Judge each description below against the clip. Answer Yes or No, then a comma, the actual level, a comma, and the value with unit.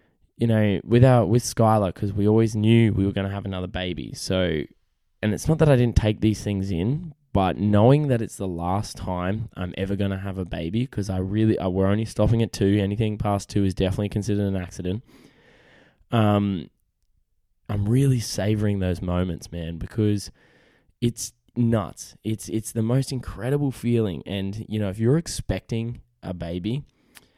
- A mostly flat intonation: No, average, 3.4 semitones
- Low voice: Yes, low, 105 Hz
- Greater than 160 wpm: Yes, average, 180 wpm